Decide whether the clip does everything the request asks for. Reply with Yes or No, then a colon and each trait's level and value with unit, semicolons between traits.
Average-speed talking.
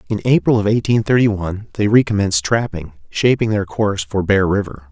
Yes: average, 185 wpm